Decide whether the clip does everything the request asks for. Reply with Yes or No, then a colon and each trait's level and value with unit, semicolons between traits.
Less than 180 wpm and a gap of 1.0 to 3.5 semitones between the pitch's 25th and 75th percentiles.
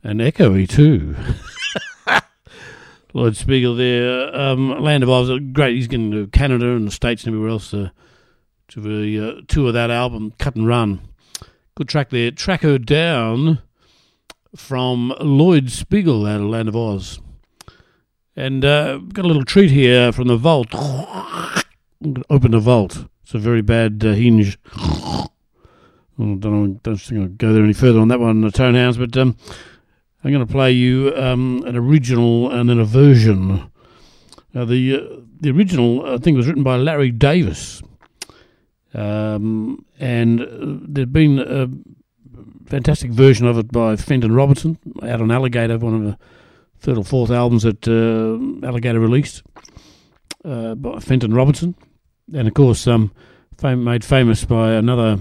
Yes: average, 160 wpm; average, 3.2 semitones